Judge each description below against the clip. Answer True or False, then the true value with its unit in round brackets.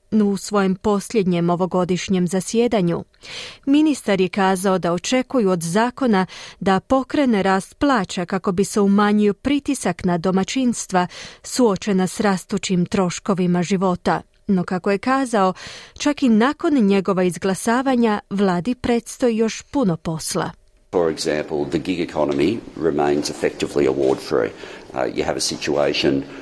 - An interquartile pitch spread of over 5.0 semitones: False (4.1 semitones)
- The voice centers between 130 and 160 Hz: False (200 Hz)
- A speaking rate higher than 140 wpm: False (125 wpm)